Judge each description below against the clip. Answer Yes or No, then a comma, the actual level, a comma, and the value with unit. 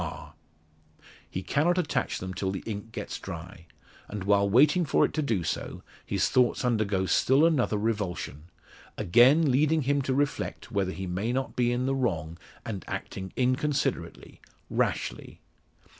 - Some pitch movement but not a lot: No, wide, 6.0 semitones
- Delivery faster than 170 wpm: No, average, 155 wpm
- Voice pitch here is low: Yes, low, 115 Hz